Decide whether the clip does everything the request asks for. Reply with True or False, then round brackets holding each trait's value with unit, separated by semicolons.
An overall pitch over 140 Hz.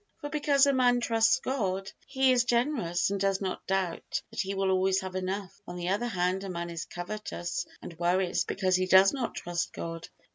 True (190 Hz)